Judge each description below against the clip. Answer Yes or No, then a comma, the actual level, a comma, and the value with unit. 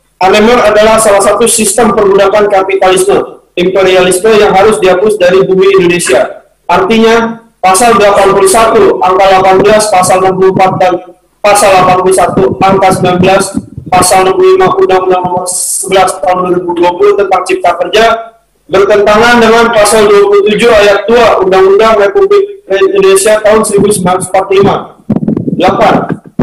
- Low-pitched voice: No, high, 195 Hz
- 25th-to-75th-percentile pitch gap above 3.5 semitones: No, narrow, 2.4 semitones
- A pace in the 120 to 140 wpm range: No, average, 105 wpm